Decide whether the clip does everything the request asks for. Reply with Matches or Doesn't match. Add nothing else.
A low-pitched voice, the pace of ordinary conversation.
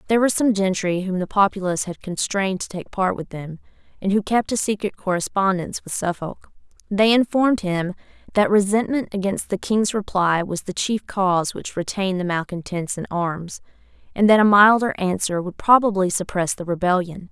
Doesn't match